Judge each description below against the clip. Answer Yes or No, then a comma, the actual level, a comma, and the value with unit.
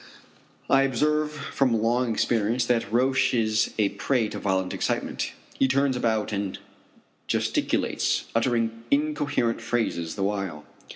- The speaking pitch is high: No, low, 115 Hz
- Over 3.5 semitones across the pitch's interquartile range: Yes, average, 4.0 semitones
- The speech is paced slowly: Yes, slow, 125 wpm